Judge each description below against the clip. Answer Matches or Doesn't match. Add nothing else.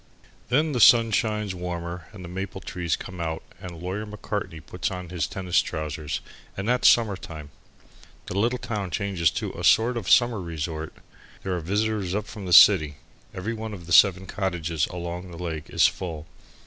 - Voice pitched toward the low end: Matches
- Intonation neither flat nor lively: Matches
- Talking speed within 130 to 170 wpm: Doesn't match